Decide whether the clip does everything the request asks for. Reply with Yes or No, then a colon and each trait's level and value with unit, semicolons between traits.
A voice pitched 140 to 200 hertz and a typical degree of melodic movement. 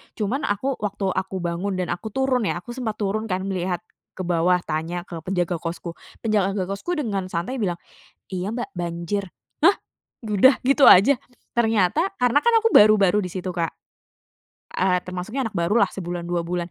Yes: high, 190 Hz; average, 3.9 semitones